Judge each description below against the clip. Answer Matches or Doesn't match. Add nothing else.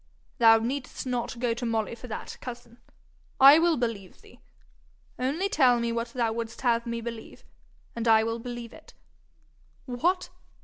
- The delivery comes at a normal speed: Matches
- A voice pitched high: Matches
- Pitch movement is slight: Matches